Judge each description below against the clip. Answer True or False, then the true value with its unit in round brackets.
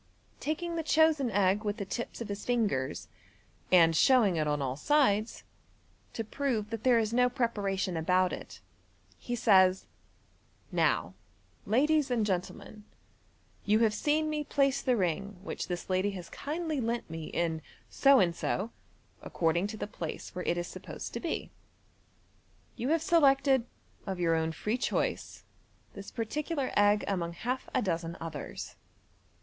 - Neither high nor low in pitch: False (210 Hz)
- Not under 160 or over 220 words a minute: True (165 wpm)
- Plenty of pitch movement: True (6.3 semitones)